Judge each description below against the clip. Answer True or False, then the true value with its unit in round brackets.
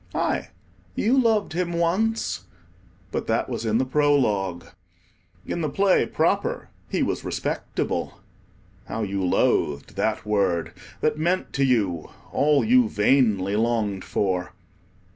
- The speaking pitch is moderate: False (115 Hz)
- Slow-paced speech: True (125 wpm)